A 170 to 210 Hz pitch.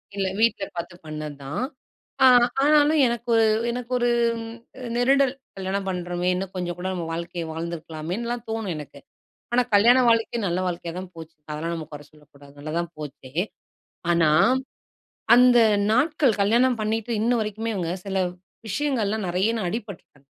Yes: high, 190 Hz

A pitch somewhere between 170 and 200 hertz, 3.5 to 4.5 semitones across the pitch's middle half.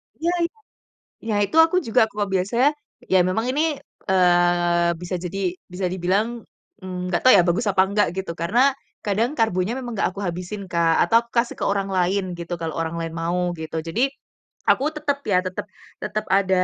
Yes: high, 190 Hz; average, 3.9 semitones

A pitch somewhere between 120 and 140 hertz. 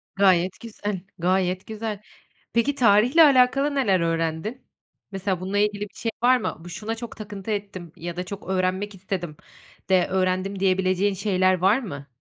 No: high, 195 Hz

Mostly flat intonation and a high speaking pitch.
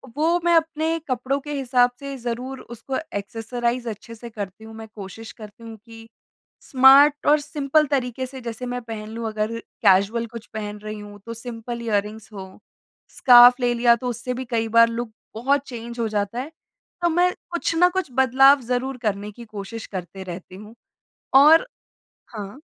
No: average, 3.4 semitones; high, 235 Hz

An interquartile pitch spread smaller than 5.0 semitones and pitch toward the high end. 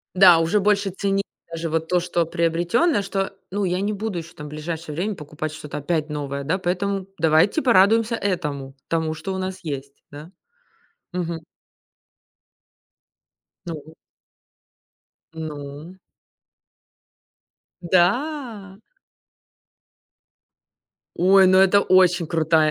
No: average, 3.7 semitones; medium, 175 Hz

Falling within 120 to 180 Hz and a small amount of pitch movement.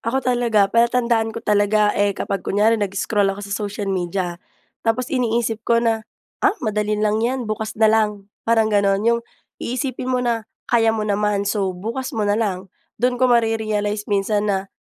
No: high, 215 Hz; narrow, 2.3 semitones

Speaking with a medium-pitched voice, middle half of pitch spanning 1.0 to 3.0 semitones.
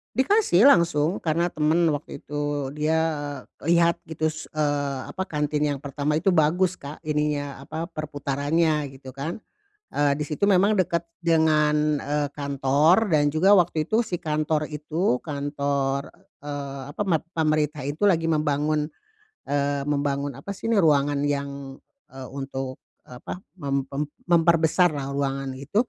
Yes: medium, 150 Hz; average, 2.7 semitones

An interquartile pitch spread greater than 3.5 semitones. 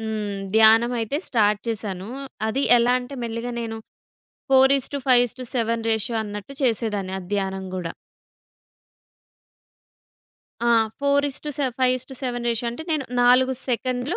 No: average, 2.8 semitones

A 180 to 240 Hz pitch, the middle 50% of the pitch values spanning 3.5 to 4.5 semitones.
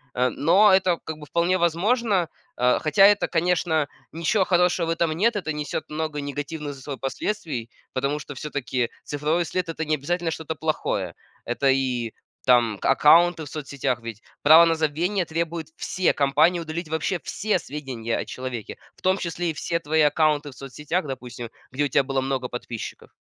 No: medium, 155 Hz; average, 3.9 semitones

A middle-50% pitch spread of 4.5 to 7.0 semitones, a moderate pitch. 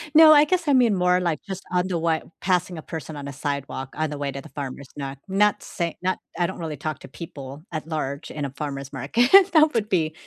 Yes: average, 5.0 semitones; medium, 160 Hz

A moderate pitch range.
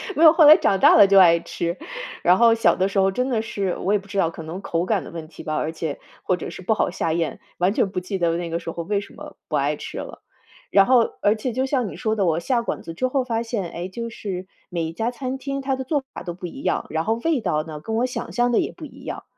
No: wide, 5.8 semitones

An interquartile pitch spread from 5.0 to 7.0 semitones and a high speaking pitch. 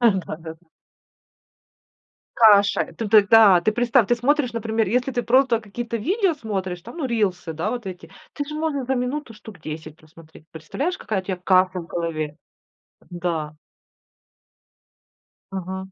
Yes: wide, 5.4 semitones; high, 210 Hz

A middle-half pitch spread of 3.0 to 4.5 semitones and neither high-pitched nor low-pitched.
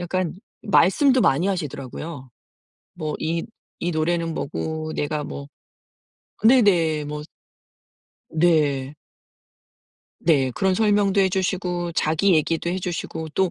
Yes: average, 3.5 semitones; medium, 170 Hz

